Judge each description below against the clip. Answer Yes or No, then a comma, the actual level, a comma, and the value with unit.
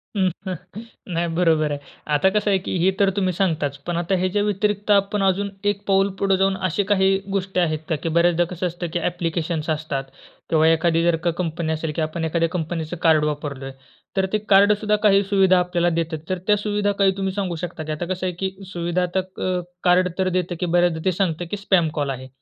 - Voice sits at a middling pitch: Yes, medium, 180 Hz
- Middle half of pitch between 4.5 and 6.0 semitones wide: No, average, 2.9 semitones